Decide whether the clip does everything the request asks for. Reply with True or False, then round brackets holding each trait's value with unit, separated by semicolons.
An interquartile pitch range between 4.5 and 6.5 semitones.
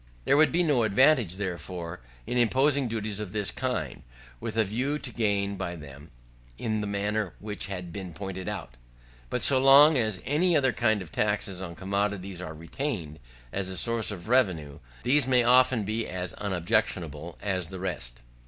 True (5.2 semitones)